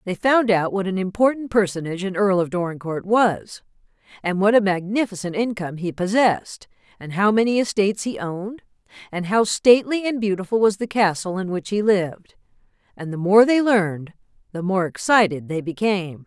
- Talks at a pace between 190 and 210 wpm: No, average, 175 wpm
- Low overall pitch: No, high, 200 Hz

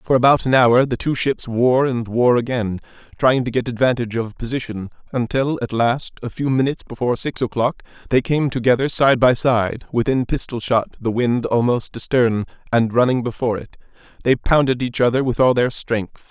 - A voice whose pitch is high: No, low, 125 Hz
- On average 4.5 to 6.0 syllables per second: Yes, 5.3 syllables/s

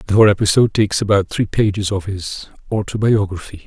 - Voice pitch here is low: Yes, low, 100 Hz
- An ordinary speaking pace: Yes, average, 165 wpm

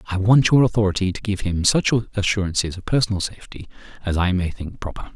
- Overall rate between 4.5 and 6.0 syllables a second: No, 6.5 syllables/s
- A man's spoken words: Yes, male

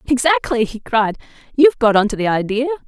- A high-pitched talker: Yes, high, 240 Hz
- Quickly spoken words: No, average, 165 wpm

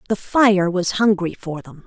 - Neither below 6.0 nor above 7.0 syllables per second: No, 4.2 syllables/s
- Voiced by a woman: Yes, female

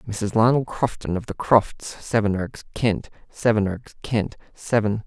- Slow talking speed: Yes, slow, 105 wpm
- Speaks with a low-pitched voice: Yes, low, 110 Hz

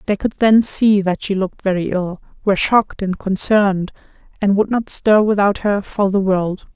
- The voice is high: Yes, high, 200 Hz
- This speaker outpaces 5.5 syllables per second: No, 5.0 syllables/s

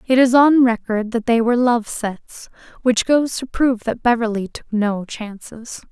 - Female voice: Yes, female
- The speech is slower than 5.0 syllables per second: Yes, 4.6 syllables/s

